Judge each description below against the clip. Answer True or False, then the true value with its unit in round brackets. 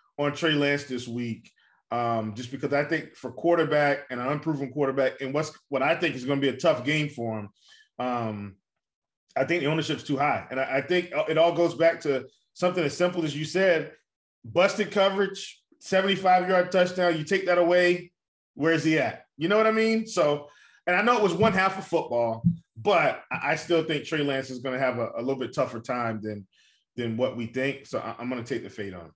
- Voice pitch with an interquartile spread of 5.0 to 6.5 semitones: True (5.6 semitones)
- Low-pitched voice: False (150 Hz)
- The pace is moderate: False (230 wpm)